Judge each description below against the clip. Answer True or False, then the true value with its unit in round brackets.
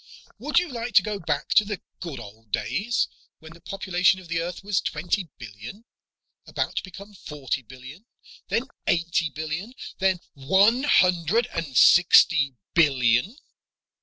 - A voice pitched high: False (175 Hz)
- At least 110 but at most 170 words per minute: True (145 wpm)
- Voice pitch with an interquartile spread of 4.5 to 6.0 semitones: True (5.5 semitones)